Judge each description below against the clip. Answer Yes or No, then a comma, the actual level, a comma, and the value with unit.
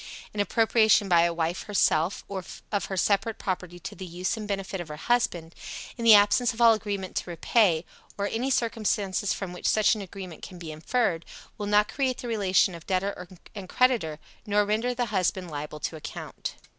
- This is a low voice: No, high, 200 Hz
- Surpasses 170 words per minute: Yes, average, 190 wpm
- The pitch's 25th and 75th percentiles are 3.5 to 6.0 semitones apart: Yes, average, 3.8 semitones